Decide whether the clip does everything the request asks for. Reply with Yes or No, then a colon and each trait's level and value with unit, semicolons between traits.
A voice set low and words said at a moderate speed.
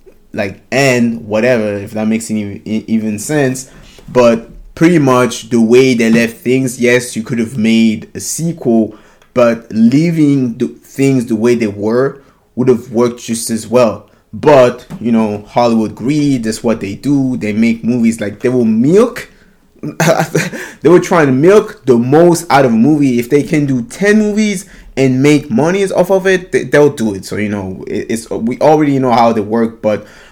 Yes: low, 120 Hz; average, 180 wpm